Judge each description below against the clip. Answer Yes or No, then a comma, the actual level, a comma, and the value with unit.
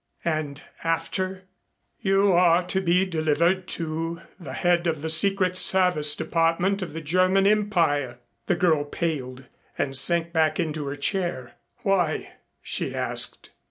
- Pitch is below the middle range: No, medium, 170 Hz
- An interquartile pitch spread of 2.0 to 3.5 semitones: Yes, average, 3.0 semitones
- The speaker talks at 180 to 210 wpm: No, average, 140 wpm